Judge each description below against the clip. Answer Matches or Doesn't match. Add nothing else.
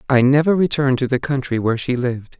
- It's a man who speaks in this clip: Matches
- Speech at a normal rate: Doesn't match